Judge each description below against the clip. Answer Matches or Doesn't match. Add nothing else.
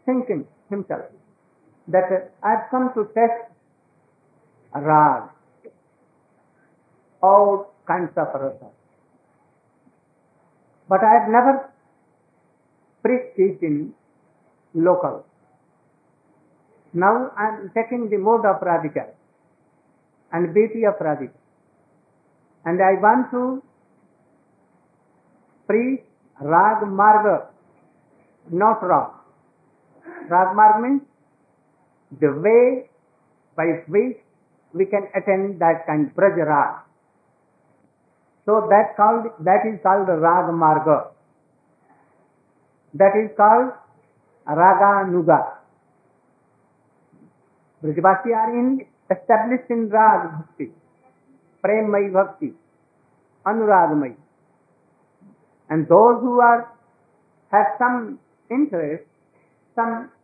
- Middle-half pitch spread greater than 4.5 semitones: Matches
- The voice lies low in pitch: Doesn't match